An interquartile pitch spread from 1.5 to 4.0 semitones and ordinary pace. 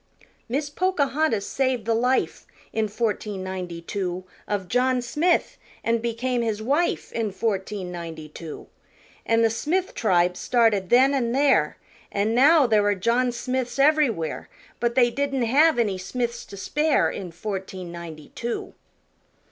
No: average, 5.3 semitones; average, 145 wpm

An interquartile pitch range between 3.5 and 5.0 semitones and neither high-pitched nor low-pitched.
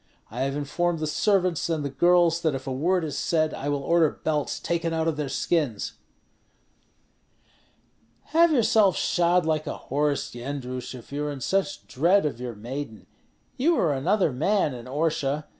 Yes: average, 4.1 semitones; medium, 155 Hz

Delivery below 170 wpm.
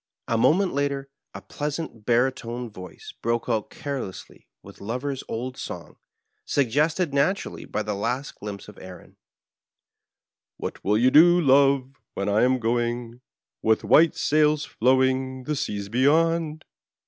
Yes: average, 140 wpm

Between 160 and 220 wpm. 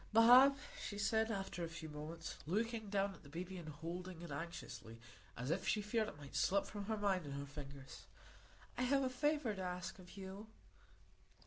Yes: average, 195 wpm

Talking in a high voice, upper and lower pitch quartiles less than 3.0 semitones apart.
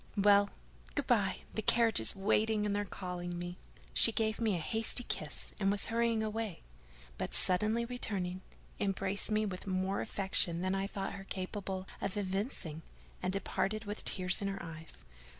Yes: high, 195 Hz; narrow, 2.6 semitones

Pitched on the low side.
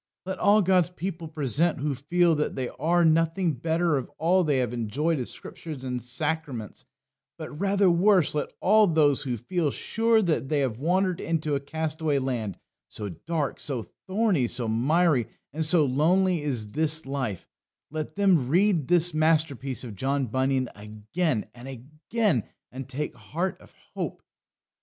No: medium, 155 Hz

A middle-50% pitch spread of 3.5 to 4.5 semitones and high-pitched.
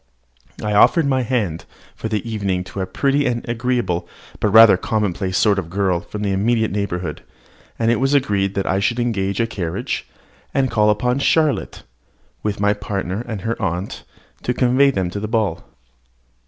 No: average, 3.8 semitones; low, 105 Hz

